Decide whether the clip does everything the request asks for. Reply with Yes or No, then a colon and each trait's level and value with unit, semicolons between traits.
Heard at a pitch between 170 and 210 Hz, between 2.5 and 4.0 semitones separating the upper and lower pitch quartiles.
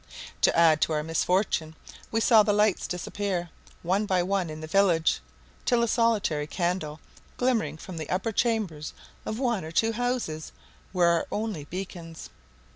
No: medium, 185 Hz; average, 5.1 semitones